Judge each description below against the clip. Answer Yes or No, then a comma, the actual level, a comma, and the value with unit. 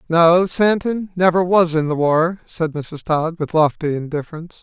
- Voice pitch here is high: No, medium, 165 Hz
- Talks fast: No, average, 170 wpm